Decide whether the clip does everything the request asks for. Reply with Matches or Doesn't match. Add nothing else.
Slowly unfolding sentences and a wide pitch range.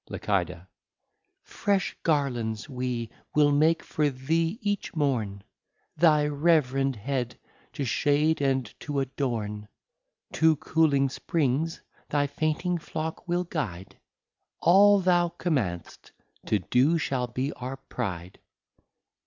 Doesn't match